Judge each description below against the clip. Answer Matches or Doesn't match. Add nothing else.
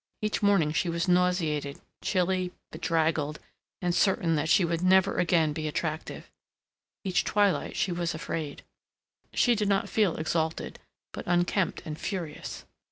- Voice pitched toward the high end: Doesn't match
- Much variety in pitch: Doesn't match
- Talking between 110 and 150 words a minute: Matches